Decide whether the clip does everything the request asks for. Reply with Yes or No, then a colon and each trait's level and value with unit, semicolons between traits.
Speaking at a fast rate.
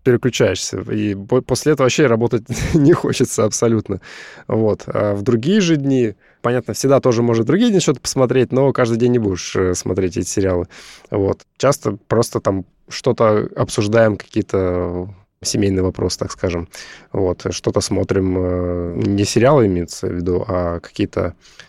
No: average, 145 wpm